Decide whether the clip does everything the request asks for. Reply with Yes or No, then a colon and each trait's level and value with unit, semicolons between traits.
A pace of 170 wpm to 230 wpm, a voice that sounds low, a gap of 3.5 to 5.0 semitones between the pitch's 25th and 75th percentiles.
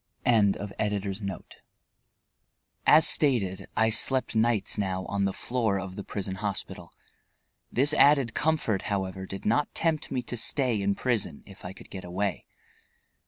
No: average, 140 wpm; low, 105 Hz; average, 4.0 semitones